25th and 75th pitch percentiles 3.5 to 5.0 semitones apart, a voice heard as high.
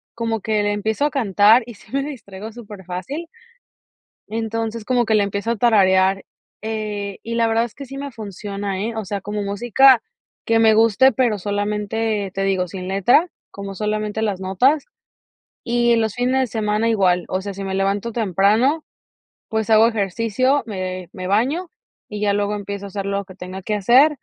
No: average, 2.7 semitones; high, 210 Hz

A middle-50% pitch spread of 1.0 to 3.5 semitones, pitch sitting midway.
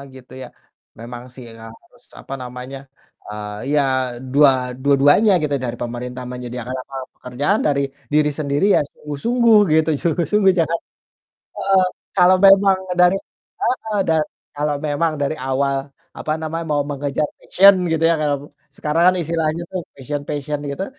No: average, 4.3 semitones; medium, 145 Hz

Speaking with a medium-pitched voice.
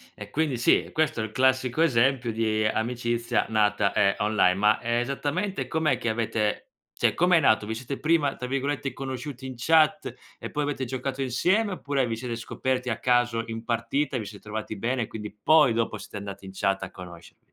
No: low, 120 Hz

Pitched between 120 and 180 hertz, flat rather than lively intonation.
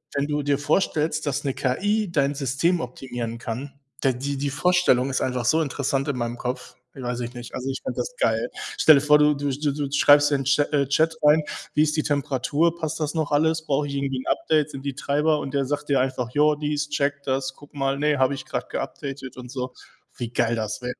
Yes: medium, 140 Hz; narrow, 2.2 semitones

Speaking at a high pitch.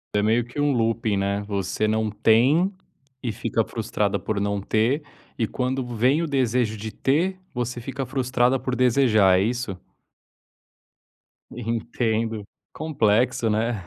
No: low, 115 Hz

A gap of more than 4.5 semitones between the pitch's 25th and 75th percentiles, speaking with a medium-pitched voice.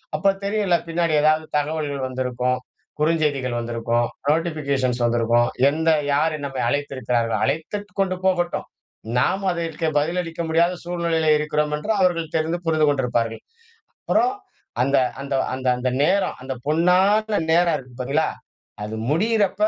Yes: average, 4.9 semitones; medium, 155 Hz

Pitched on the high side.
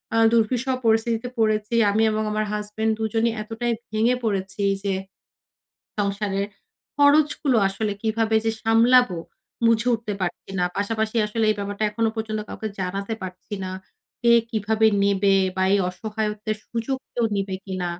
Yes: high, 220 Hz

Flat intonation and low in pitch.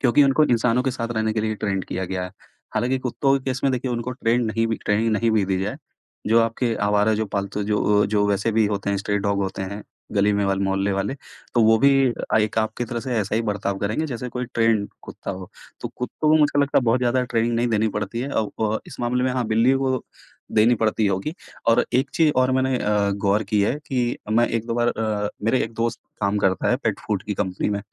No: average, 3.2 semitones; low, 110 Hz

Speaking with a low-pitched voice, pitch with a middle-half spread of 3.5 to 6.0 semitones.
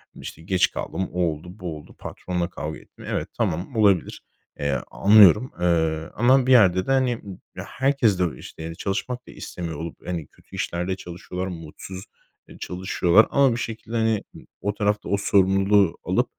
Yes: very low, 95 Hz; average, 3.8 semitones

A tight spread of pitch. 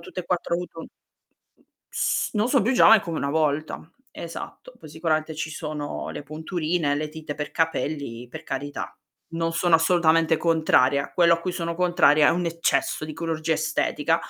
Yes: narrow, 1.8 semitones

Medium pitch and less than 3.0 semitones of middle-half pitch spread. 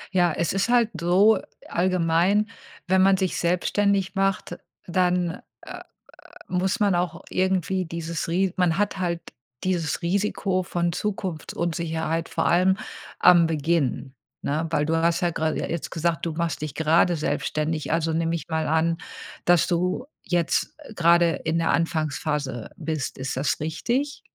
Yes: medium, 170 Hz; narrow, 2.4 semitones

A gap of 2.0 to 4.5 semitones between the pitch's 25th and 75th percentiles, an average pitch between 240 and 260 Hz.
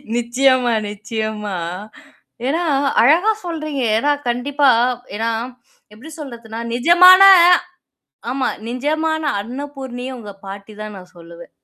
No: average, 5.0 semitones; very high, 250 Hz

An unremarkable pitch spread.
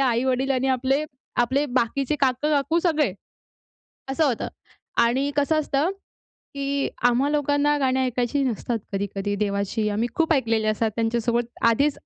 Yes: average, 3.6 semitones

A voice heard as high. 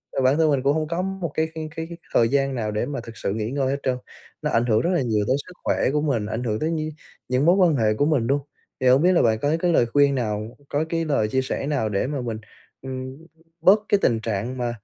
No: low, 135 Hz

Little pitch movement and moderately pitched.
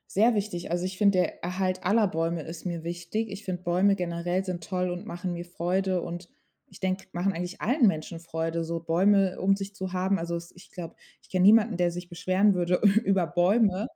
Yes: narrow, 2.1 semitones; medium, 180 Hz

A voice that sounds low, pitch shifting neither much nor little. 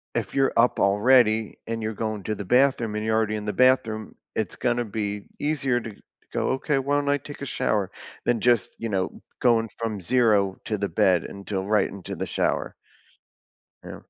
Yes: low, 110 Hz; average, 3.1 semitones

